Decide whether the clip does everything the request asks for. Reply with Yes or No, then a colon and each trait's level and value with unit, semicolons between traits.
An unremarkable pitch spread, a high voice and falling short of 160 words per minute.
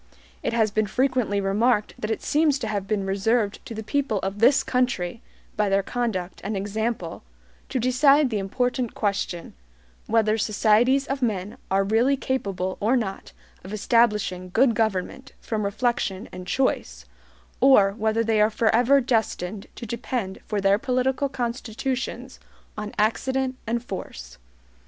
Yes: average, 3.9 semitones; high, 220 Hz; average, 145 wpm